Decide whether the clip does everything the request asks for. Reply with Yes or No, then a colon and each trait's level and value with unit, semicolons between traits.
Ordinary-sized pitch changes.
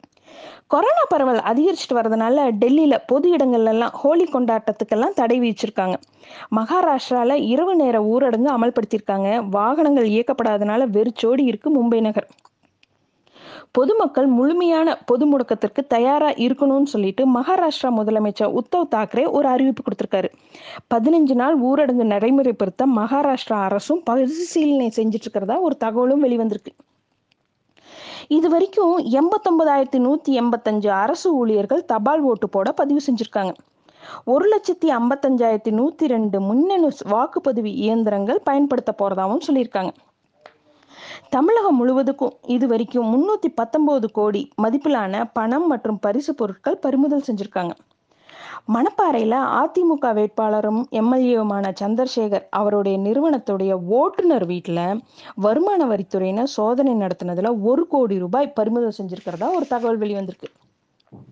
Yes: average, 4.7 semitones